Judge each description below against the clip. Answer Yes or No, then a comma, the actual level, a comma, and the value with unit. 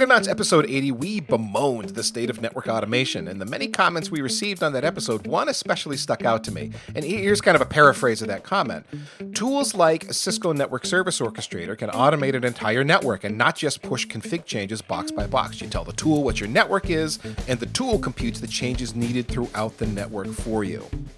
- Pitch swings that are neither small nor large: No, wide, 7.8 semitones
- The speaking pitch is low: Yes, low, 130 Hz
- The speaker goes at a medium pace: No, fast, 215 wpm